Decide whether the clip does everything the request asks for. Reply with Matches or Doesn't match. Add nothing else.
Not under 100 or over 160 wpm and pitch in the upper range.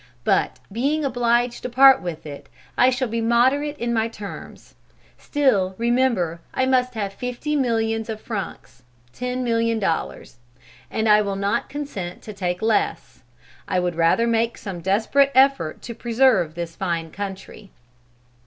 Matches